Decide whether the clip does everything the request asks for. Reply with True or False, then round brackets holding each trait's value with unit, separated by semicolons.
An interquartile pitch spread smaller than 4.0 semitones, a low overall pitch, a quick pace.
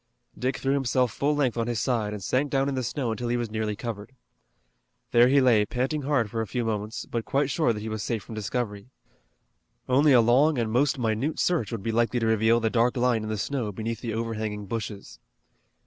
True (2.9 semitones; 115 Hz; 225 wpm)